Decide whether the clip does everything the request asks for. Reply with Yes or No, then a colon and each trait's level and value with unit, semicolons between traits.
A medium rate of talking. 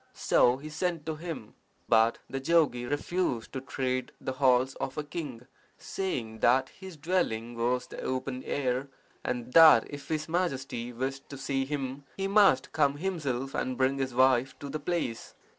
Yes: average, 170 wpm